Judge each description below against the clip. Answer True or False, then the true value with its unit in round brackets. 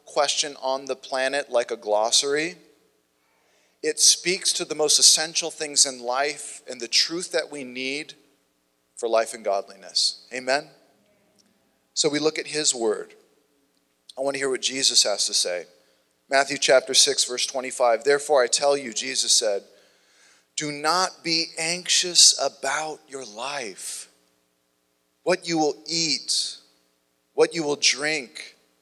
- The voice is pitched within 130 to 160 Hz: True (140 Hz)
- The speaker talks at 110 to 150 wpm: True (140 wpm)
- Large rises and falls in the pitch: False (4.6 semitones)